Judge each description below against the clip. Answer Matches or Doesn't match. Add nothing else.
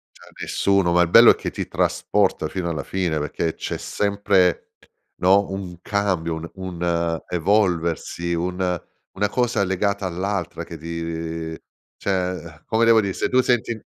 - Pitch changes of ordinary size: Matches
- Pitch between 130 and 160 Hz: Doesn't match